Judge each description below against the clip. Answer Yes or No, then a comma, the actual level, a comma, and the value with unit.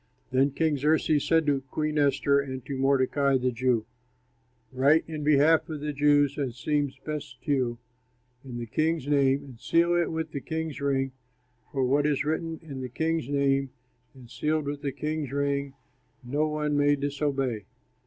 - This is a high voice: No, medium, 140 Hz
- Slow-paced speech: No, average, 175 wpm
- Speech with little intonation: Yes, narrow, 2.2 semitones